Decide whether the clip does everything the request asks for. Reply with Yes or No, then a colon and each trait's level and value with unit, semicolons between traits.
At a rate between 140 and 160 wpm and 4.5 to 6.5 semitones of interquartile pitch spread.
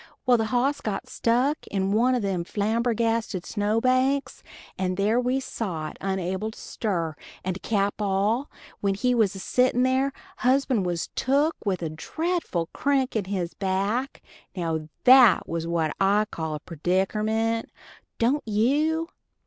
Yes: average, 155 wpm; average, 5.1 semitones